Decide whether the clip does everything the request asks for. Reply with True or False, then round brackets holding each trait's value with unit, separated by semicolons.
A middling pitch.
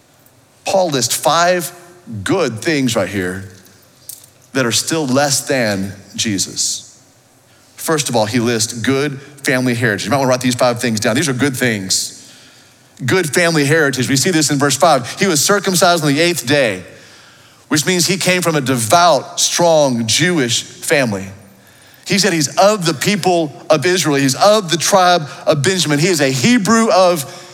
True (145 Hz)